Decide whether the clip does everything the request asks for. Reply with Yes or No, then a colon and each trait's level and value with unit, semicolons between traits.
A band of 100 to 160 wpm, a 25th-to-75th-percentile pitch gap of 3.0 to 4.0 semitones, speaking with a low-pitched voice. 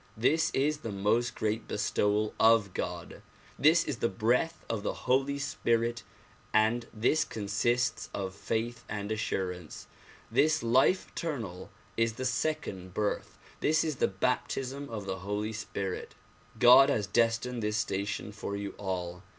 Yes: average, 140 wpm; average, 3.7 semitones; low, 110 Hz